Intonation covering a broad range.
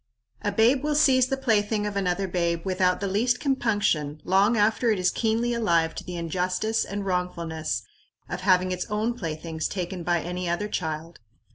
No: average, 4.2 semitones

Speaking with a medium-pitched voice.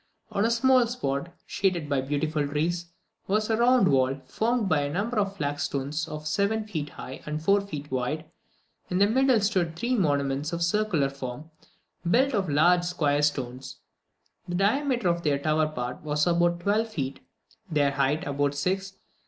Yes: medium, 165 Hz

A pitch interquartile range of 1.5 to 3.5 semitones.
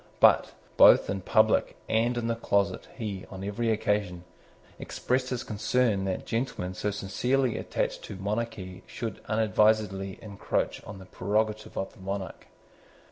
Yes: average, 2.9 semitones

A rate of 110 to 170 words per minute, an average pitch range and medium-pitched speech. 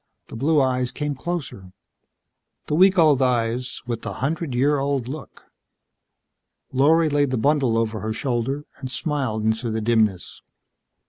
No: average, 145 wpm; average, 4.3 semitones; low, 130 Hz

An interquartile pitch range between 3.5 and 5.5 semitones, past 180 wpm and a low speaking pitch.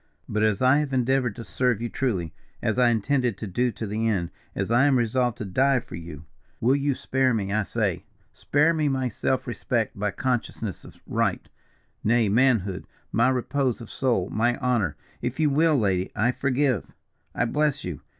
Yes: average, 3.9 semitones; average, 190 wpm; low, 120 Hz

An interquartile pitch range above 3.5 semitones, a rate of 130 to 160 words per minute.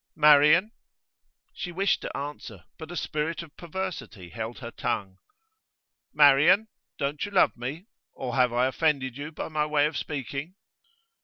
Yes: average, 4.1 semitones; average, 150 wpm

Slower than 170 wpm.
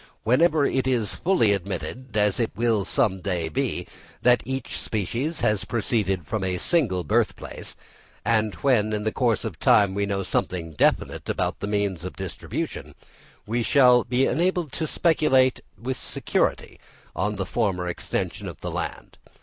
Yes: average, 160 wpm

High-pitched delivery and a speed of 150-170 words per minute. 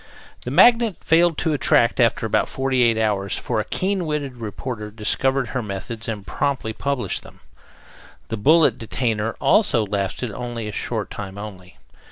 No: low, 115 Hz; average, 160 wpm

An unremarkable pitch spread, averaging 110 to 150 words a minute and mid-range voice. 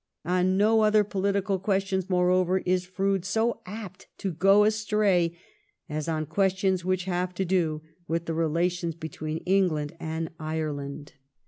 Yes: average, 3.1 semitones; average, 140 wpm; medium, 180 Hz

